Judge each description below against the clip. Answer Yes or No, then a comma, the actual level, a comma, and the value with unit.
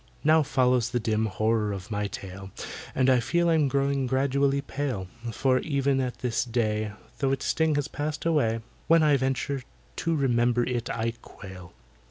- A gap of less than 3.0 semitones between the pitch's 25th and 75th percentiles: No, average, 3.7 semitones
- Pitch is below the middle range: Yes, low, 130 Hz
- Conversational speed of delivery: Yes, average, 170 wpm